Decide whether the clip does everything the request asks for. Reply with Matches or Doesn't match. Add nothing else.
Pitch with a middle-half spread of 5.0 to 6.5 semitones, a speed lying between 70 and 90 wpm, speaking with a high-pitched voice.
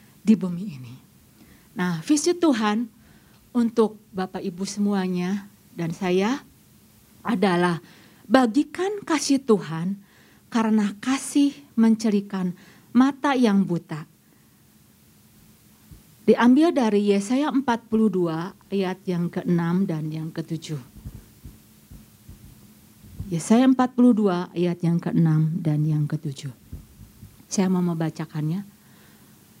Matches